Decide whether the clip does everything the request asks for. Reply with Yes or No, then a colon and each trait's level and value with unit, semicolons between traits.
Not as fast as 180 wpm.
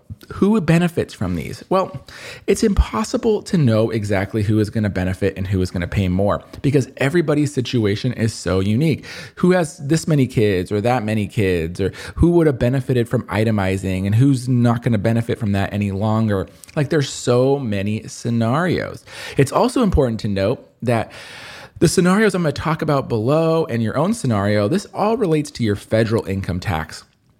No: average, 185 wpm